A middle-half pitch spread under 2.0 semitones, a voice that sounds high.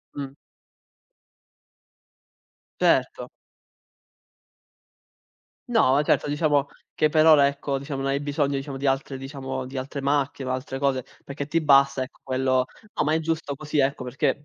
No: narrow, 1.5 semitones; medium, 140 Hz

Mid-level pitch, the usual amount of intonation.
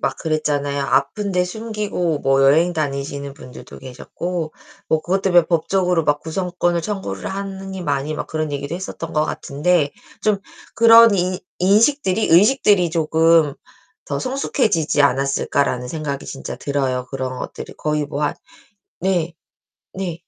Yes: medium, 165 Hz; average, 4.9 semitones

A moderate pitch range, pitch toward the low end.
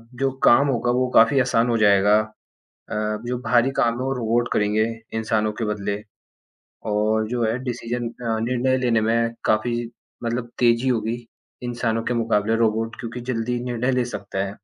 No: narrow, 1.9 semitones; low, 115 Hz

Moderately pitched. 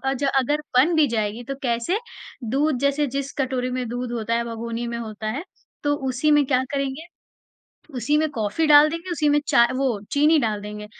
No: very high, 260 Hz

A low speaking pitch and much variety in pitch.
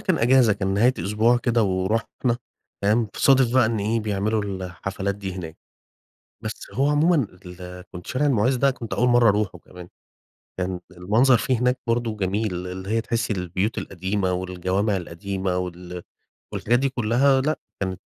No: low, 105 Hz; average, 4.5 semitones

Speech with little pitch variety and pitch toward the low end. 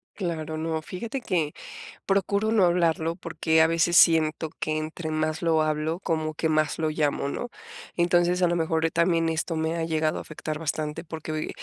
No: narrow, 1.6 semitones; medium, 160 Hz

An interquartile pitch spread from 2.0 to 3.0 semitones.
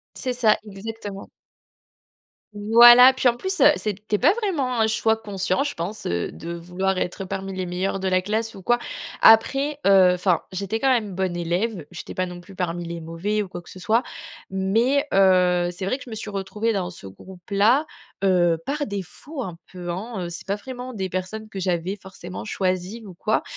No: average, 3.7 semitones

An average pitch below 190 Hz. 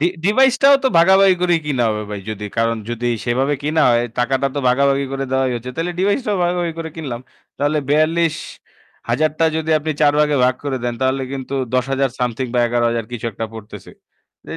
Yes: medium, 140 Hz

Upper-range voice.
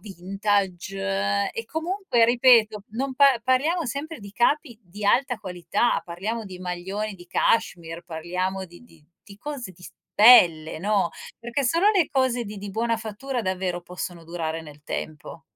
Yes: high, 205 Hz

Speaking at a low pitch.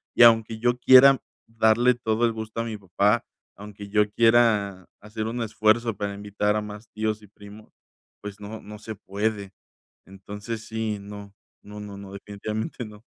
Yes: low, 105 Hz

